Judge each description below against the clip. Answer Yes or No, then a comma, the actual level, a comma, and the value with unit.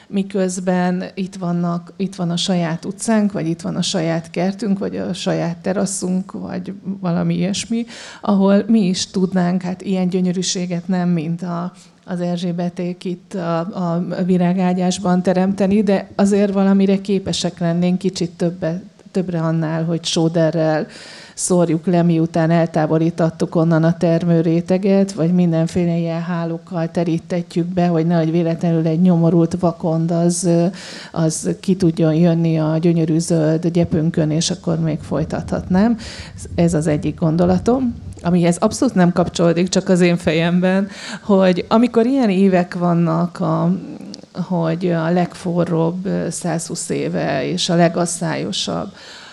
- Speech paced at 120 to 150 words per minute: Yes, average, 130 wpm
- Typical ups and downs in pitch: No, narrow, 2.0 semitones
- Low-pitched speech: No, medium, 175 Hz